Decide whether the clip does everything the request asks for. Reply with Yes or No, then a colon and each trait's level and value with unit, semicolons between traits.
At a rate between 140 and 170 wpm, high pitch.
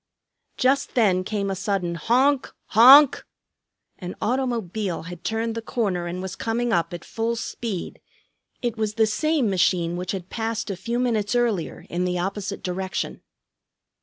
Yes: average, 155 wpm; high, 210 Hz